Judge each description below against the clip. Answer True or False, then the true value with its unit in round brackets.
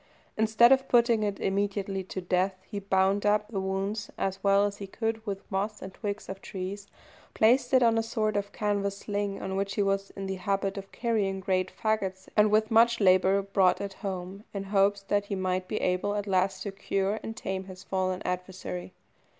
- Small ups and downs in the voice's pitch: True (1.7 semitones)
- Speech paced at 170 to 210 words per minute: True (200 wpm)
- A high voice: True (195 Hz)